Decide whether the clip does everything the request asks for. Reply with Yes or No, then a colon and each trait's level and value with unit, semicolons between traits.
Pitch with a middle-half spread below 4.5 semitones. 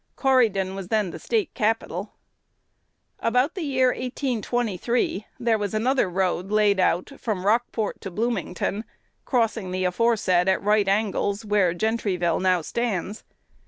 Yes: average, 3.9 semitones